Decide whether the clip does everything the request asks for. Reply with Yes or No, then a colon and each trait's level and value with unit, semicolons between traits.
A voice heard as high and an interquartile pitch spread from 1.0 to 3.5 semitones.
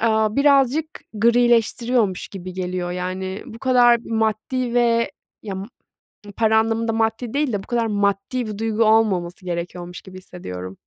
No: high, 220 Hz; average, 4.0 semitones